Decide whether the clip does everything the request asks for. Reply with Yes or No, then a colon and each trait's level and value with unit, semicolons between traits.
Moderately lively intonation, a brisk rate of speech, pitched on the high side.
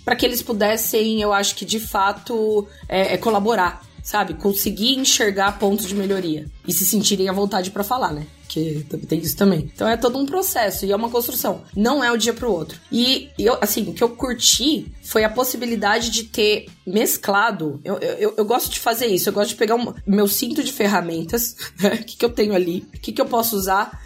Yes: average, 3.3 semitones; fast, 220 wpm; high, 210 Hz